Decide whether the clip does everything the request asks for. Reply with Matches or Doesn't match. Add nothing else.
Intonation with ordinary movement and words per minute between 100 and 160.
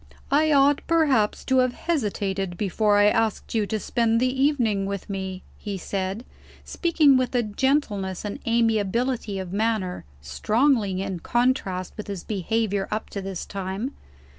Matches